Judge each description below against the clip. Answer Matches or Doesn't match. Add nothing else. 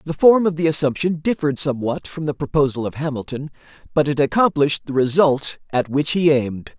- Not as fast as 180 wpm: Doesn't match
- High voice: Doesn't match